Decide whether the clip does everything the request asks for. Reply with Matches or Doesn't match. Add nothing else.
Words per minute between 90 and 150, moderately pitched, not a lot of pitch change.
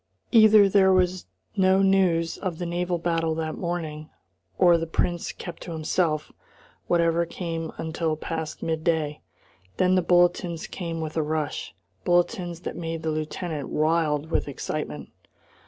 Matches